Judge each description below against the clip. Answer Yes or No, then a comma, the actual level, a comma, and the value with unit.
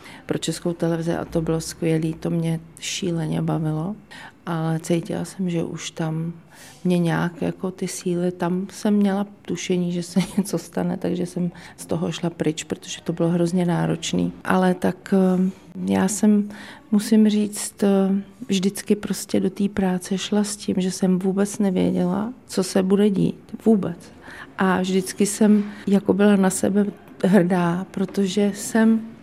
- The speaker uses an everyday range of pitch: Yes, average, 3.0 semitones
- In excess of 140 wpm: Yes, average, 150 wpm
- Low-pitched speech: No, medium, 185 Hz